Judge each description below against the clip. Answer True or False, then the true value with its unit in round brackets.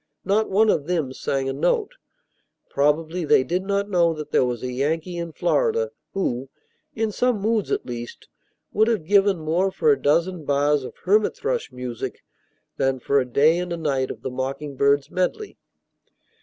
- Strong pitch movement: True (6.3 semitones)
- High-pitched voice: False (165 Hz)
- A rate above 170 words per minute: True (180 wpm)